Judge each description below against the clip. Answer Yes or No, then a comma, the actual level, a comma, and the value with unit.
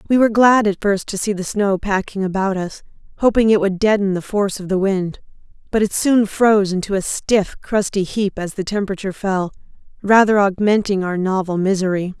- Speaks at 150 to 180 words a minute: No, average, 190 wpm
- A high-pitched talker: Yes, high, 200 Hz